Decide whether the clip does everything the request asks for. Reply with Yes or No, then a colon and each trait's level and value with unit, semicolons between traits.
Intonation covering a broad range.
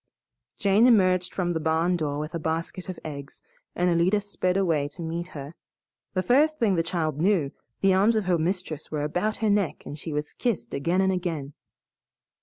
No: average, 3.6 semitones